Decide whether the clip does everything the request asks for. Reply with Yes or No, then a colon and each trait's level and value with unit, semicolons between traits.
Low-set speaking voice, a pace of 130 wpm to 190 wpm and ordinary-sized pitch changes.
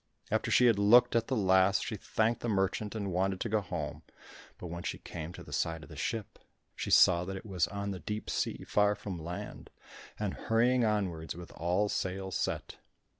No: very low, 95 Hz; fast, 205 wpm; average, 3.3 semitones